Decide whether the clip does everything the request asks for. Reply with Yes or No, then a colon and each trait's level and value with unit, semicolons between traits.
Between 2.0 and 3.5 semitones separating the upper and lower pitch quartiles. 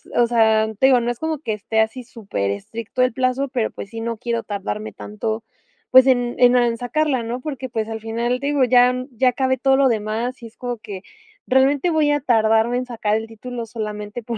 Yes: narrow, 2.5 semitones